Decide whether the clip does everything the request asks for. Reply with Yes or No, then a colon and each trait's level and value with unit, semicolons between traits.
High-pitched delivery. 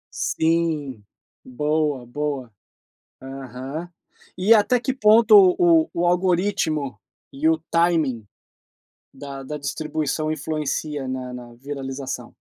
No: medium, 150 Hz